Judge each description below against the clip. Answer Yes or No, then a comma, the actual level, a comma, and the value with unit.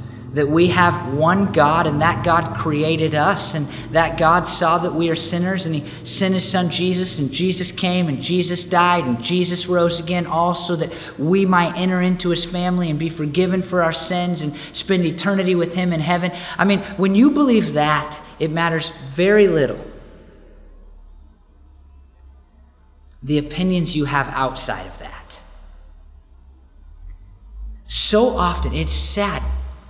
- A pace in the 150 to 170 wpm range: Yes, average, 155 wpm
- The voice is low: No, medium, 165 Hz